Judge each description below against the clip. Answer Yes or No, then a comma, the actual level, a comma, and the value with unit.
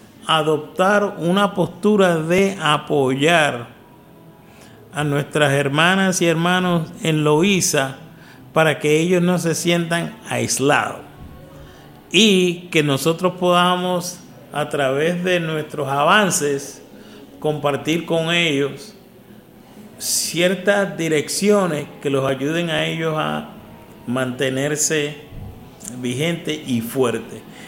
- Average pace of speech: No, slow, 95 wpm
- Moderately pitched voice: Yes, medium, 160 Hz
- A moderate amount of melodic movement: Yes, average, 3.6 semitones